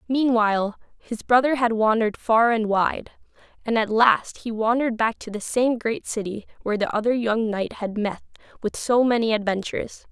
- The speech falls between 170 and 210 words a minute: Yes, average, 180 wpm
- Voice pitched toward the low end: No, high, 225 Hz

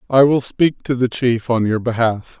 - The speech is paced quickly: Yes, fast, 225 wpm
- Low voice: Yes, low, 120 Hz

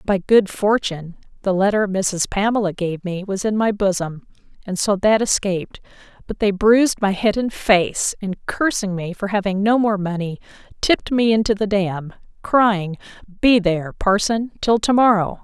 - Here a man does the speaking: No, female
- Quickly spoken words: No, average, 170 wpm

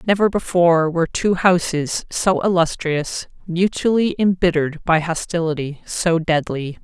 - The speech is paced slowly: Yes, slow, 115 wpm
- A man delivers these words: No, female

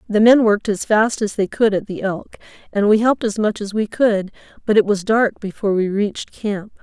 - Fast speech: Yes, fast, 235 wpm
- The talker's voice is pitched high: Yes, high, 210 Hz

